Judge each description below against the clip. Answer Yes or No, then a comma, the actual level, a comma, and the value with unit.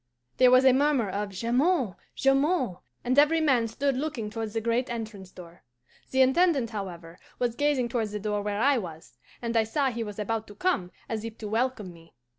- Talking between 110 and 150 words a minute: No, average, 200 wpm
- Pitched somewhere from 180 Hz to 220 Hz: No, high, 230 Hz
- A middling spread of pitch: Yes, average, 4.1 semitones